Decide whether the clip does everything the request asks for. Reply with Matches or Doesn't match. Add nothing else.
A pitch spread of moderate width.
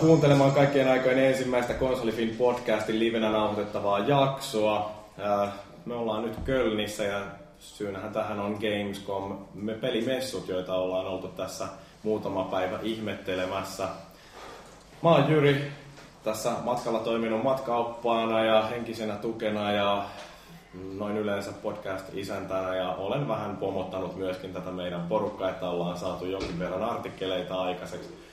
Matches